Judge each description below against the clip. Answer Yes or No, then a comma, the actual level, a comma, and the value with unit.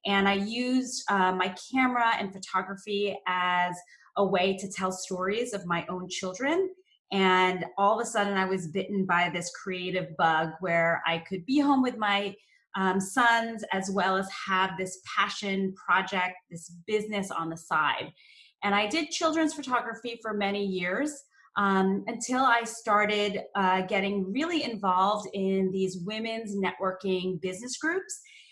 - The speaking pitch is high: Yes, high, 195 Hz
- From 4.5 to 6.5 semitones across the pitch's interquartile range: No, average, 3.7 semitones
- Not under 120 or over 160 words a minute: Yes, average, 155 wpm